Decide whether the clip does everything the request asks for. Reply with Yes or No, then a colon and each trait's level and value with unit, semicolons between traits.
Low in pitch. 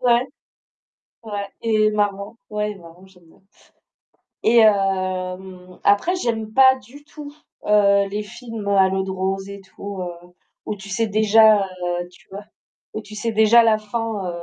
No: high, 205 Hz